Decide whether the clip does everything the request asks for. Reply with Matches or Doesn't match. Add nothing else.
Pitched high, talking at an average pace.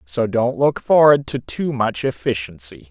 Doesn't match